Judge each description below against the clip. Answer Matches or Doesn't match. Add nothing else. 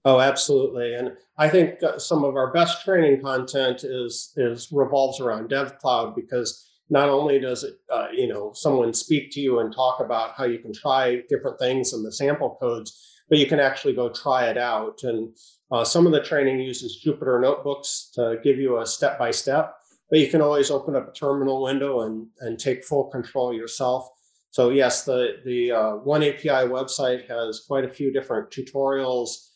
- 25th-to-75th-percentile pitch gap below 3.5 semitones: Matches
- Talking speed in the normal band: Matches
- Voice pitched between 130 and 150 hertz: Matches